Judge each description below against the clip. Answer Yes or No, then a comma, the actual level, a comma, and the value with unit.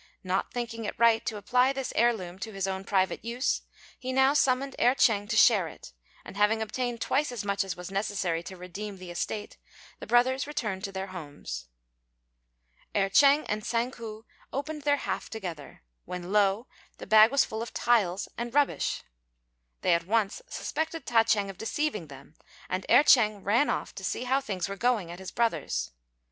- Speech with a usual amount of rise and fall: Yes, average, 4.4 semitones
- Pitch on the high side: Yes, high, 215 Hz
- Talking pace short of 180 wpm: No, average, 190 wpm